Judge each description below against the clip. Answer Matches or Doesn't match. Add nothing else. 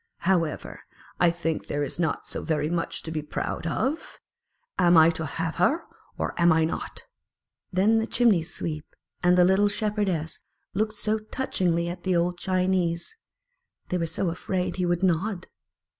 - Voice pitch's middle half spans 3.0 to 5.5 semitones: Doesn't match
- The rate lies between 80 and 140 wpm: Doesn't match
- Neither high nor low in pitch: Matches